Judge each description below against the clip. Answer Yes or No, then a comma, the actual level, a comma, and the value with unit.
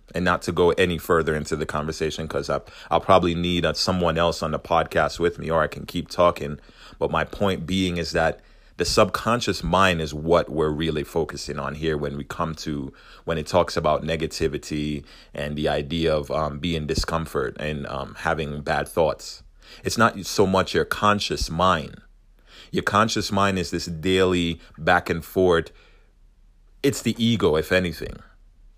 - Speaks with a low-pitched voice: Yes, very low, 80 Hz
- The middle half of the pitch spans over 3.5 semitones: No, narrow, 2.5 semitones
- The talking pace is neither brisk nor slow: Yes, average, 175 wpm